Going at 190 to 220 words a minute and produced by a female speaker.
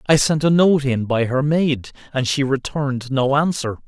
No: average, 200 wpm; male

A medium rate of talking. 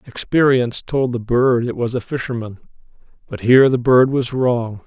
Yes: average, 175 wpm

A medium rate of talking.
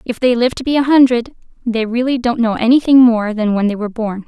No: fast, 255 wpm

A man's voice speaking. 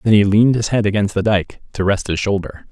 Yes: male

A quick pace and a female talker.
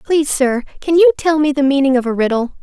Yes: fast, 250 wpm; female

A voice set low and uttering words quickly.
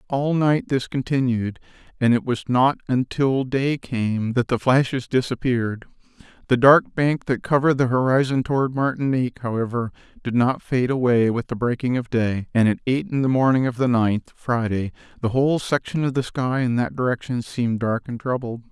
No: low, 125 Hz; average, 185 wpm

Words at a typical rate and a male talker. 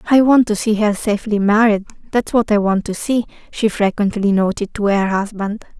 No: average, 185 wpm; female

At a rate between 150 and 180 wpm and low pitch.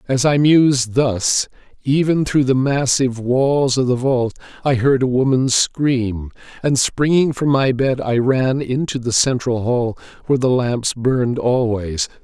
Yes: average, 160 wpm; low, 130 Hz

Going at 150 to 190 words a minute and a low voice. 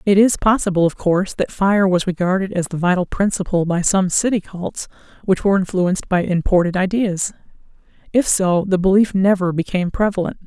No: average, 170 wpm; high, 190 Hz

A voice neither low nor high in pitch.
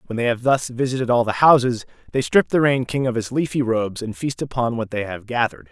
No: low, 120 Hz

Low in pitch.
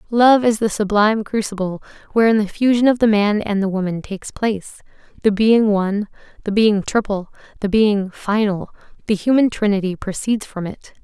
No: high, 210 Hz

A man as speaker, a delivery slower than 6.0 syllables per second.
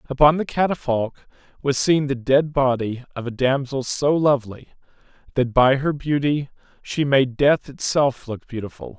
Yes: male; 4.7 syllables/s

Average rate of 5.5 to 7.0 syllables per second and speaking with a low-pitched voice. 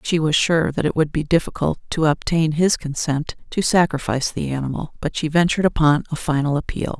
No: 5.7 syllables/s; medium, 155 Hz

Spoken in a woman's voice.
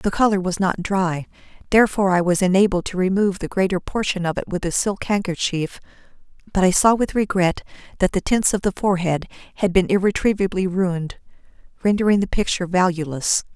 Yes: female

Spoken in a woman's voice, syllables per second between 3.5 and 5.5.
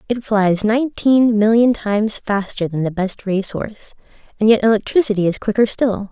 Yes: female; 5.1 syllables/s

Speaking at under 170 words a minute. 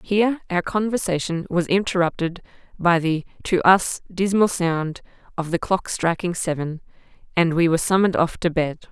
Yes: average, 155 wpm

